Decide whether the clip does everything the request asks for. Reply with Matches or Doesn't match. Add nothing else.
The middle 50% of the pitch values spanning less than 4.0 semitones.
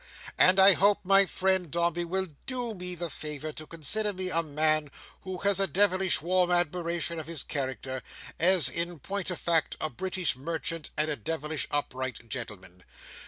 Matches